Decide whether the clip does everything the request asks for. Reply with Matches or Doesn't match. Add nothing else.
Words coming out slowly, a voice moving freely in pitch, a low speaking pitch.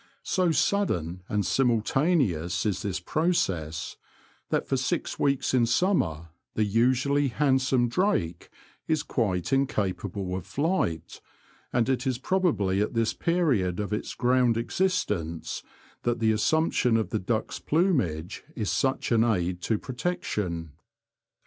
Matches